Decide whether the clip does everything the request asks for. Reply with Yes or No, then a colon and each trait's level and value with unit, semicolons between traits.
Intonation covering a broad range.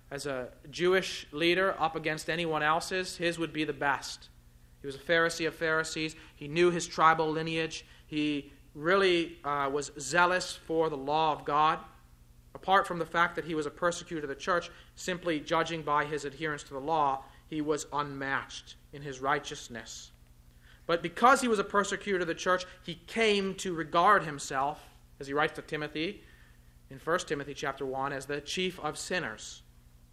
No: average, 3.5 semitones